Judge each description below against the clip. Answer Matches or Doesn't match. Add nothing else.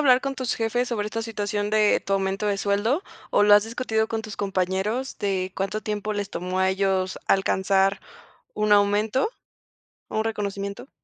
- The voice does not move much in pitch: Matches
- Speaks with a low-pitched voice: Doesn't match